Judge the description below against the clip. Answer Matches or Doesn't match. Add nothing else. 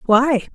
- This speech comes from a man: Doesn't match